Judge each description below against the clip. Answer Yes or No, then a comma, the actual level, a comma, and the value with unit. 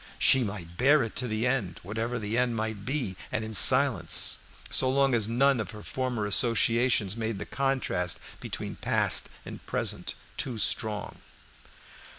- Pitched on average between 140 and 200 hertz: No, low, 115 Hz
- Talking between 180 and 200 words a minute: No, average, 160 wpm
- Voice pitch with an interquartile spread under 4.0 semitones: Yes, average, 3.5 semitones